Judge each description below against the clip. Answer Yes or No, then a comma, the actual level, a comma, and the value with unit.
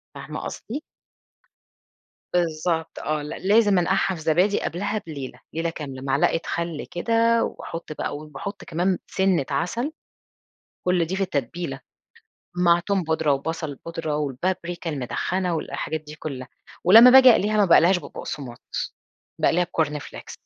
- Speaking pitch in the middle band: Yes, medium, 170 Hz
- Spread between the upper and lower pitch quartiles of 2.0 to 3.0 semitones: No, average, 3.9 semitones